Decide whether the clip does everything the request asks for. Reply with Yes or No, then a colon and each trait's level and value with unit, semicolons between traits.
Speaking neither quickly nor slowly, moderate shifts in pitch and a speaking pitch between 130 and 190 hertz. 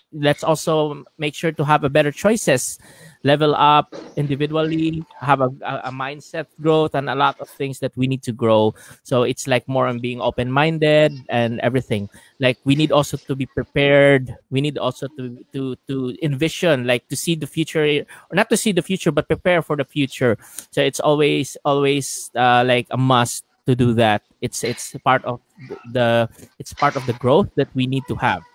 Yes: average, 195 wpm; average, 3.3 semitones; medium, 140 Hz